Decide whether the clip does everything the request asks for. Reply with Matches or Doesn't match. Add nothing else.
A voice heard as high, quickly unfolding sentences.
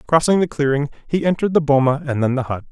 Doesn't match